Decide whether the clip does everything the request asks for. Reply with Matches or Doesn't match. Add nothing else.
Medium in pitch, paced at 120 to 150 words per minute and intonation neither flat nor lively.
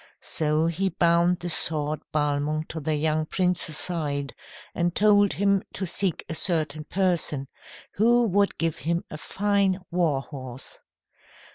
Matches